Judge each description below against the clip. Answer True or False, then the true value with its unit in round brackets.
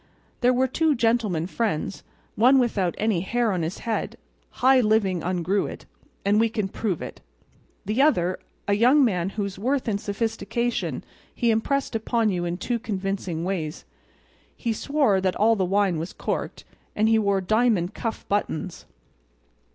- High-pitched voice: True (210 Hz)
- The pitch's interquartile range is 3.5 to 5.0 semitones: True (4.0 semitones)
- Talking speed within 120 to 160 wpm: True (145 wpm)